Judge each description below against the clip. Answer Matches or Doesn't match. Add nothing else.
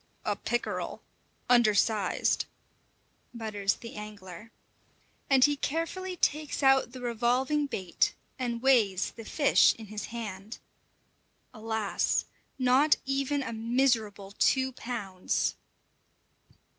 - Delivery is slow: Matches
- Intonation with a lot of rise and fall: Doesn't match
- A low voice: Doesn't match